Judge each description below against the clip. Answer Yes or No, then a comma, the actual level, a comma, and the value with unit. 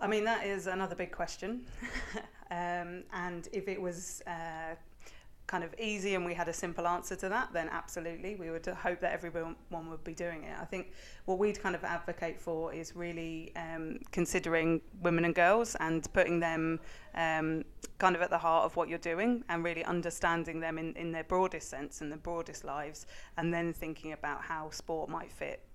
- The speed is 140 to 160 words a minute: No, average, 195 wpm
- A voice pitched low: No, medium, 170 Hz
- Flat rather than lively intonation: Yes, narrow, 2.0 semitones